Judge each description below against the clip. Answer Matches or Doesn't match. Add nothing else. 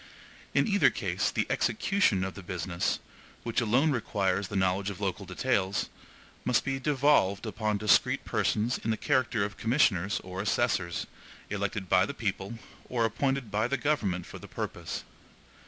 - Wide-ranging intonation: Doesn't match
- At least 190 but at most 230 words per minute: Doesn't match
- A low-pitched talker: Matches